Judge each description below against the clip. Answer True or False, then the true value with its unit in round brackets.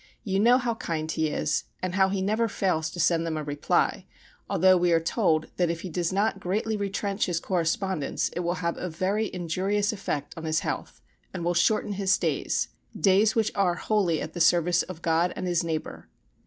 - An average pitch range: True (3.1 semitones)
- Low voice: False (180 Hz)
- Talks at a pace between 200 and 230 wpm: True (205 wpm)